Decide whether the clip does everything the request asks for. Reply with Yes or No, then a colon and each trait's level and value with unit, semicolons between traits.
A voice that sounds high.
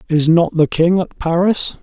No: medium, 170 Hz